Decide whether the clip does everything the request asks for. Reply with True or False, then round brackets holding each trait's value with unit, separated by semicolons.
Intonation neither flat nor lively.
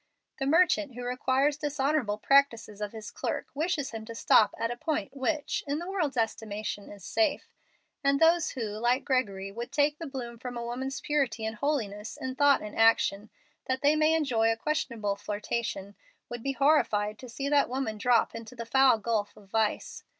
True (4.5 semitones)